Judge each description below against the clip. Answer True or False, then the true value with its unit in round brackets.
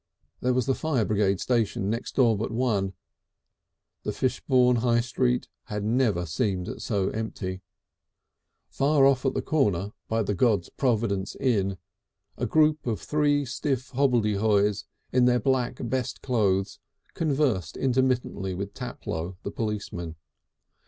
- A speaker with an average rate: False (130 wpm)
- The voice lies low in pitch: True (115 Hz)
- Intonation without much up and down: False (4.4 semitones)